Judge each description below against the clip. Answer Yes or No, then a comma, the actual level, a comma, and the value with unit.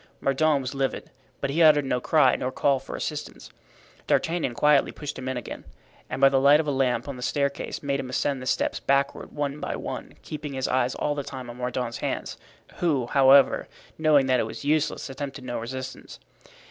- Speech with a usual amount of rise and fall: No, narrow, 2.2 semitones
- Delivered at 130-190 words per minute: No, average, 200 wpm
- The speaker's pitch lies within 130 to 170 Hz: Yes, low, 135 Hz